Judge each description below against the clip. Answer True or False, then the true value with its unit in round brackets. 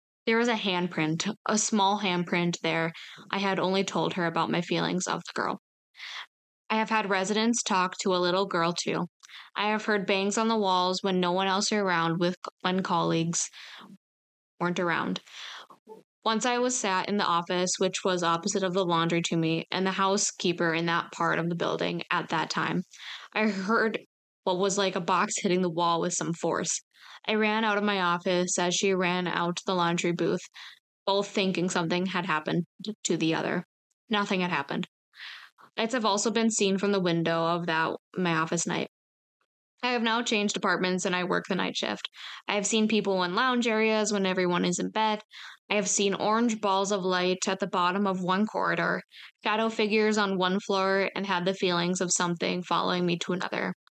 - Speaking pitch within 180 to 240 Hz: True (190 Hz)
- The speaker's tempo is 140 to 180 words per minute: False (195 wpm)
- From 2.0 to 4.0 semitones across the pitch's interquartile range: True (2.9 semitones)